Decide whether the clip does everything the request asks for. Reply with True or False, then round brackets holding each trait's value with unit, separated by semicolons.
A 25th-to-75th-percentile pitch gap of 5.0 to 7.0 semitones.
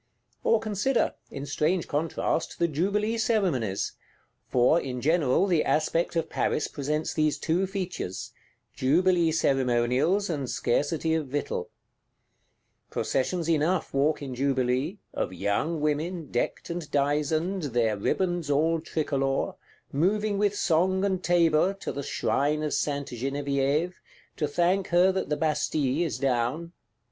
False (4.2 semitones)